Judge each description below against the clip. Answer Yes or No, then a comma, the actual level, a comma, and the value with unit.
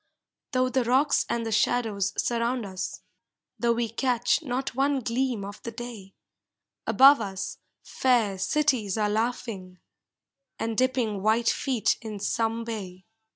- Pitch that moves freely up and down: No, average, 3.4 semitones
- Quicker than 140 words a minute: No, slow, 135 wpm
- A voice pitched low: No, high, 230 Hz